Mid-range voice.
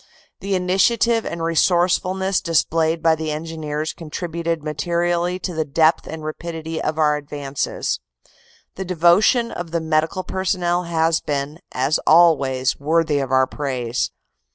Yes: medium, 165 Hz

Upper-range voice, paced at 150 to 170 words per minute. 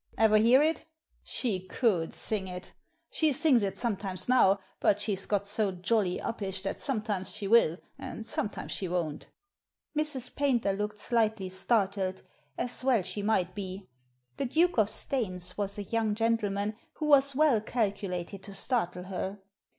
Yes: high, 210 Hz; average, 155 wpm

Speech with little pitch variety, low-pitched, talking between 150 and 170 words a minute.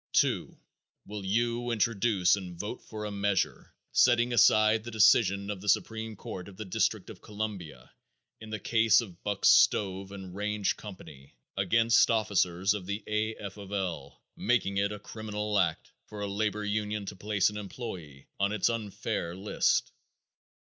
Yes: narrow, 2.1 semitones; low, 105 Hz; average, 165 wpm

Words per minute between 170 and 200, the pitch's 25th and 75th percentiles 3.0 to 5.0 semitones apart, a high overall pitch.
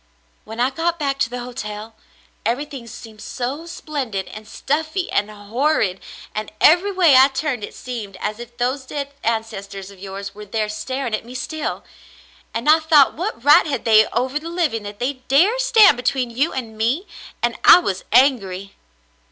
No: average, 180 wpm; wide, 5.4 semitones; very high, 250 Hz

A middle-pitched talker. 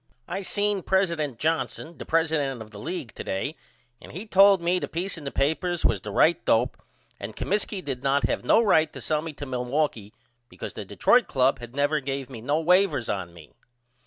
Yes: medium, 150 Hz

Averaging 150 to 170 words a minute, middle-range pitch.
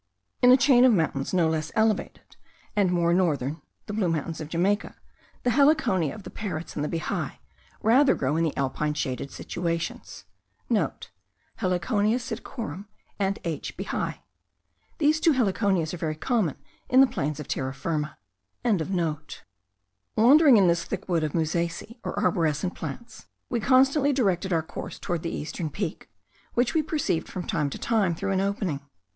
Yes: average, 160 wpm; medium, 180 Hz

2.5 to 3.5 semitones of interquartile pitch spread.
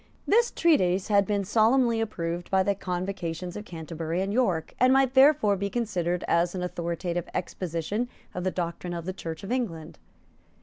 No: average, 4.2 semitones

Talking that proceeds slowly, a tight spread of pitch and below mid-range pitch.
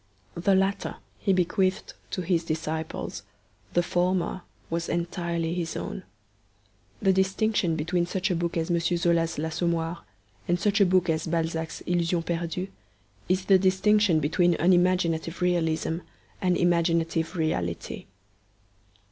No: slow, 125 wpm; narrow, 2.0 semitones; medium, 175 Hz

